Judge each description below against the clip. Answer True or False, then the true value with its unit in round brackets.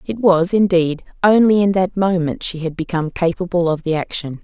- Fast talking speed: False (190 wpm)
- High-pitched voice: False (175 Hz)